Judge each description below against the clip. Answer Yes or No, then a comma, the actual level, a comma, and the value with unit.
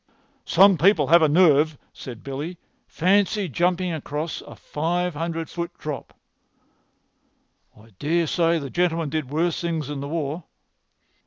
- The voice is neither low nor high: Yes, medium, 165 Hz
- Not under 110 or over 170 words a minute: Yes, average, 140 wpm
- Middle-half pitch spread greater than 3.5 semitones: No, average, 2.9 semitones